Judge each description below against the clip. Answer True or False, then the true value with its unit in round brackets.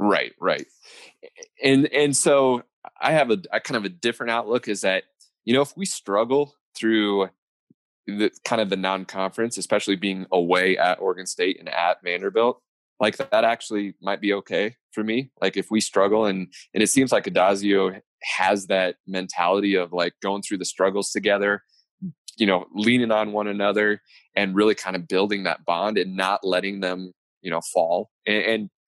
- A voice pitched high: False (105 Hz)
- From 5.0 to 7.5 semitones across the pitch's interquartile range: False (3.6 semitones)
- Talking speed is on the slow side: False (185 wpm)